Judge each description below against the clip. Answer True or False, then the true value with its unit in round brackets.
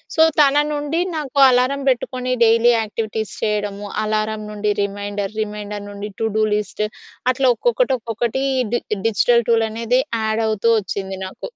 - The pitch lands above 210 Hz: True (220 Hz)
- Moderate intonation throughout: True (3.2 semitones)